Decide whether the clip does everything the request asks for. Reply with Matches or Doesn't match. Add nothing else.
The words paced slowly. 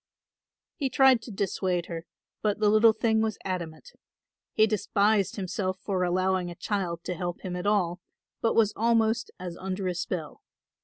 Doesn't match